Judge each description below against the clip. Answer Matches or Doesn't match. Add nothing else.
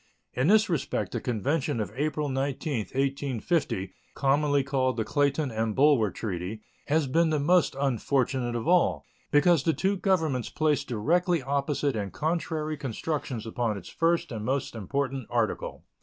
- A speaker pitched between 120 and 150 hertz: Matches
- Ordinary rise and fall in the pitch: Matches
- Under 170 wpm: Matches